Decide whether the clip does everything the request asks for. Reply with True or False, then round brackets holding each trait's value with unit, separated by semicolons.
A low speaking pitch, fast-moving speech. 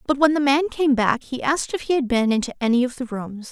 False (265 Hz; 290 wpm)